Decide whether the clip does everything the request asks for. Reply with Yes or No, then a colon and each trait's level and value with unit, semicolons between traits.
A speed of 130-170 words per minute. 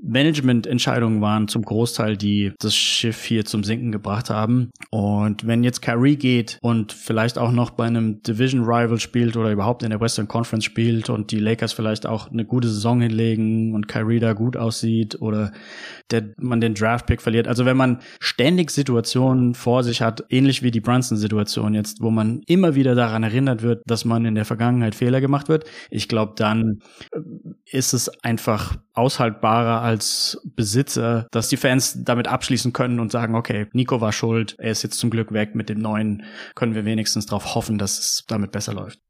No: average, 185 wpm